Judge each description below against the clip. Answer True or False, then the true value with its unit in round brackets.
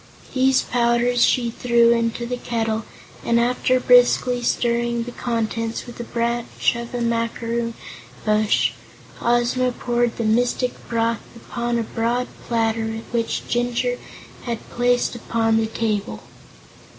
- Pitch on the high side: True (235 Hz)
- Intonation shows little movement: True (1.0 semitones)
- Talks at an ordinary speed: False (125 wpm)